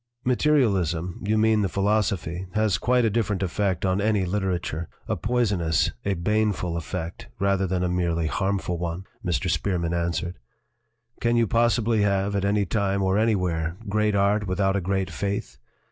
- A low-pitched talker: Yes, very low, 95 Hz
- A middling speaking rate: Yes, average, 165 wpm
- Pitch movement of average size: Yes, average, 3.2 semitones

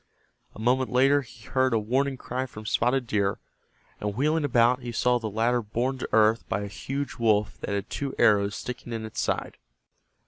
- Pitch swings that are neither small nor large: Yes, average, 3.4 semitones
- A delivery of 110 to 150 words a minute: No, average, 195 wpm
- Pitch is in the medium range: No, low, 120 Hz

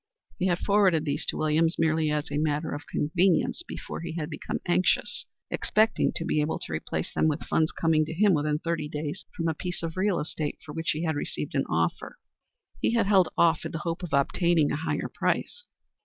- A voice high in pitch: No, medium, 160 Hz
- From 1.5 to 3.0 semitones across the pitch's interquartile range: Yes, narrow, 2.6 semitones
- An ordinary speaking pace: No, fast, 215 wpm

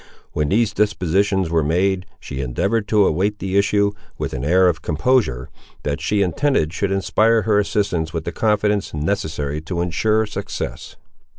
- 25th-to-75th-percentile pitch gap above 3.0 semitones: Yes, average, 4.6 semitones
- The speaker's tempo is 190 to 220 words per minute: No, average, 160 wpm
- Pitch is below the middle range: Yes, very low, 95 Hz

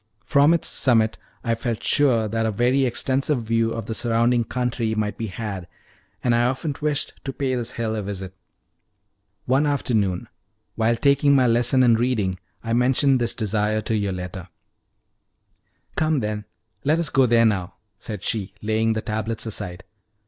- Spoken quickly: No, average, 165 wpm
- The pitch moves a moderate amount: Yes, average, 3.1 semitones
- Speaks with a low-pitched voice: Yes, low, 115 Hz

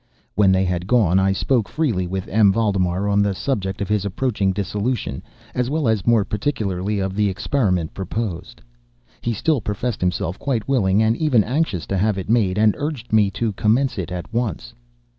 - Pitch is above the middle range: No, low, 105 Hz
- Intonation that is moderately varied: Yes, average, 3.7 semitones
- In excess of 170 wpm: Yes, average, 185 wpm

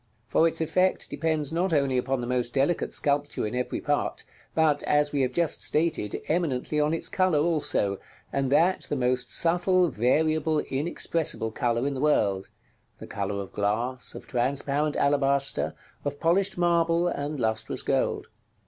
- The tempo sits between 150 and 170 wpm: Yes, average, 155 wpm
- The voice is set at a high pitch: No, medium, 145 Hz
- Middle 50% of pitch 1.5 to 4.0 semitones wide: No, average, 4.5 semitones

